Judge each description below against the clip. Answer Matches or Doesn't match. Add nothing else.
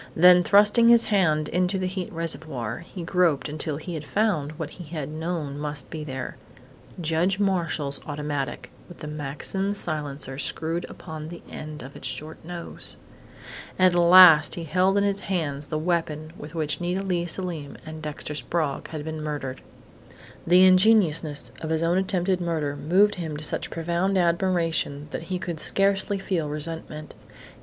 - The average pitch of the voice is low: Doesn't match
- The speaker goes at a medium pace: Matches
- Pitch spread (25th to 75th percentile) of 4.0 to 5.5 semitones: Doesn't match